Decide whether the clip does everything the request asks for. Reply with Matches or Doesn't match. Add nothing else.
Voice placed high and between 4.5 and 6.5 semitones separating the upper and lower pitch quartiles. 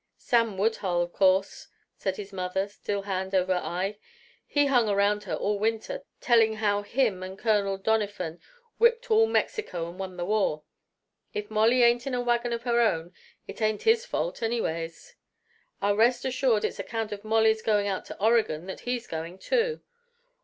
Doesn't match